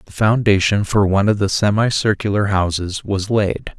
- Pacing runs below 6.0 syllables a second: Yes, 5.0 syllables/s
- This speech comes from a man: Yes, male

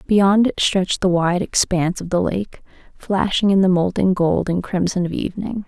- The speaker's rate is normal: Yes, average, 190 wpm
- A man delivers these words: No, female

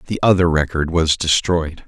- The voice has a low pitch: Yes, very low, 85 Hz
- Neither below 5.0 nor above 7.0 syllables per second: No, 4.8 syllables/s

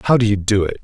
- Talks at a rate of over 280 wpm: Yes, fast, 360 wpm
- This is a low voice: Yes, low, 105 Hz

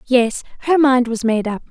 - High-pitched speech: Yes, high, 245 Hz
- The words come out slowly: No, fast, 210 wpm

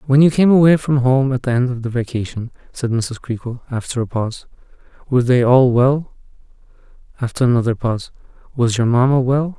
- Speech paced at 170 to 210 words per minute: Yes, average, 180 wpm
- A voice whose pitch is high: No, low, 125 Hz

